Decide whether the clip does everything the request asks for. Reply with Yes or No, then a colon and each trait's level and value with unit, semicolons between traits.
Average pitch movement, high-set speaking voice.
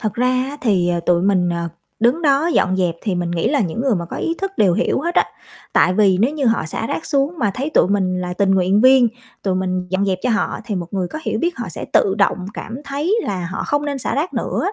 No: wide, 7.0 semitones; high, 205 Hz